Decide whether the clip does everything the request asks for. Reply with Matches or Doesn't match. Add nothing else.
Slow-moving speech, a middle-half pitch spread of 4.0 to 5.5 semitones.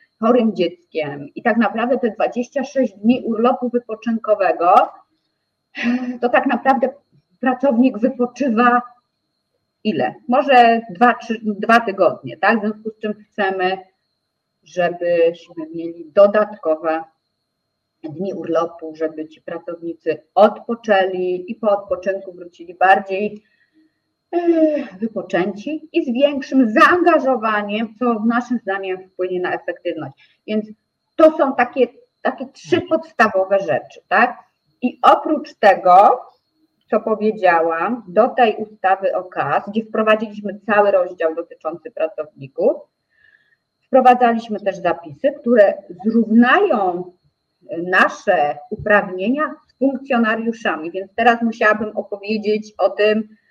Matches